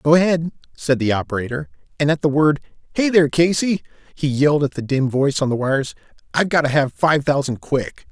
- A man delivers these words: Yes, male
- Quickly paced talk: No, average, 190 wpm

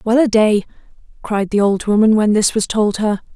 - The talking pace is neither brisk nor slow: No, fast, 215 wpm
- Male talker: No, female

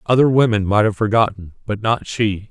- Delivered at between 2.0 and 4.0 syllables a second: No, 5.3 syllables/s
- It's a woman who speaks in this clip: No, male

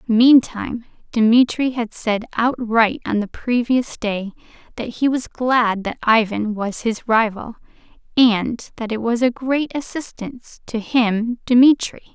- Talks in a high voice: Yes, high, 230 Hz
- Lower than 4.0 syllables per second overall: Yes, 3.8 syllables/s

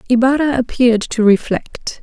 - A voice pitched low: No, high, 245 Hz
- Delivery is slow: Yes, slow, 120 wpm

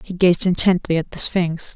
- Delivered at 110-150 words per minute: No, fast, 205 wpm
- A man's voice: No, female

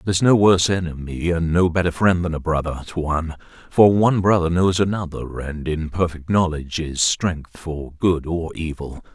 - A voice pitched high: No, very low, 85 Hz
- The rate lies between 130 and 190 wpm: Yes, average, 175 wpm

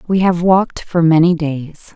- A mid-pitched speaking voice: Yes, medium, 170 Hz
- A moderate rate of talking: Yes, average, 185 wpm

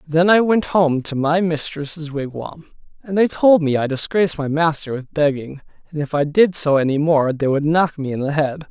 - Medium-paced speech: No, fast, 220 wpm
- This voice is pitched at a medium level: Yes, medium, 155 Hz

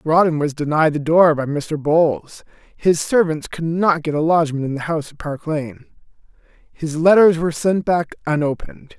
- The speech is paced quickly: No, average, 180 wpm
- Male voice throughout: Yes, male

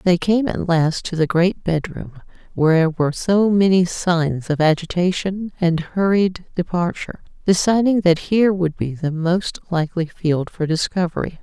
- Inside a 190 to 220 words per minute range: No, average, 150 wpm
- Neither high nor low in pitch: Yes, medium, 175 Hz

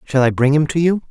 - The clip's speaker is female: No, male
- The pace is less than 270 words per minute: No, fast, 325 wpm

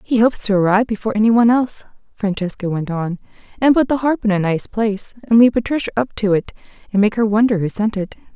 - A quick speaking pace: Yes, fast, 230 wpm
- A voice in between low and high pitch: No, high, 215 Hz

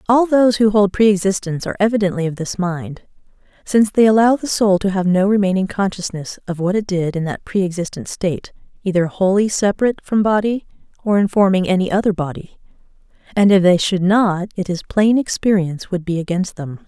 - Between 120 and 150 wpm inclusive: No, average, 190 wpm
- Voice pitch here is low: No, high, 195 Hz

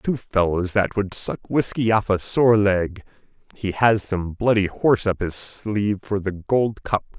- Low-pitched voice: Yes, low, 100 Hz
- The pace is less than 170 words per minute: No, average, 185 wpm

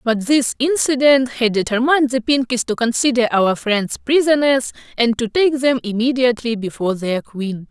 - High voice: Yes, high, 245 Hz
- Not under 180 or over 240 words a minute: No, average, 155 wpm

